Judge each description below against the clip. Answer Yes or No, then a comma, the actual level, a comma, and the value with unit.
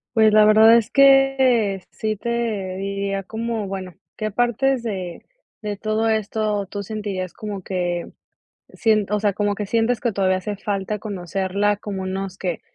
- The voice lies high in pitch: Yes, high, 210 Hz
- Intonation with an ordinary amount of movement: No, narrow, 2.3 semitones